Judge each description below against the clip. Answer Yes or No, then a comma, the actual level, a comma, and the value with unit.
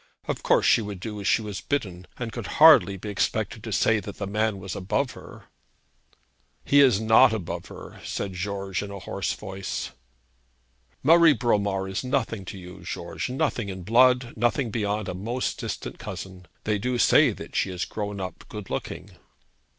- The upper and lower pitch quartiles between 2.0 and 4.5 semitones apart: Yes, average, 3.8 semitones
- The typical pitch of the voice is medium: No, low, 105 Hz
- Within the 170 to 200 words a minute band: Yes, average, 180 wpm